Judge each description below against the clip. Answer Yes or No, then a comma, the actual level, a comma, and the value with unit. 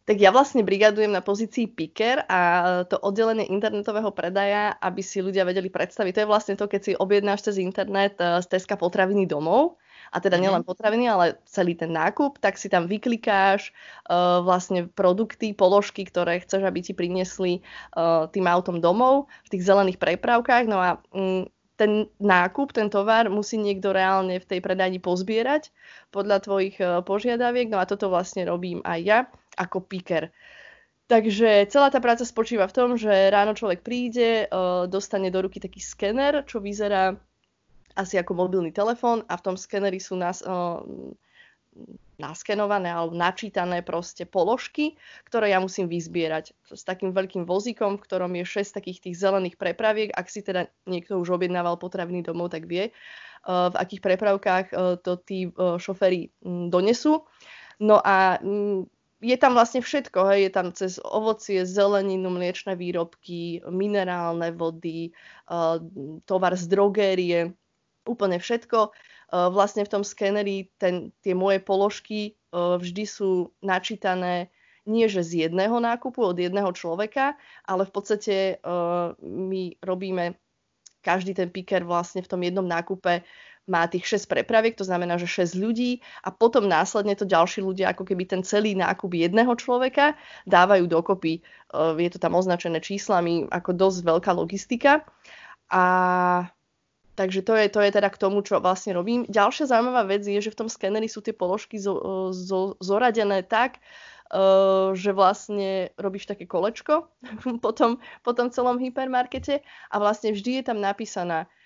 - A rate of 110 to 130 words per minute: No, average, 155 wpm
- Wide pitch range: No, average, 2.9 semitones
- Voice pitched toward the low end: No, high, 195 Hz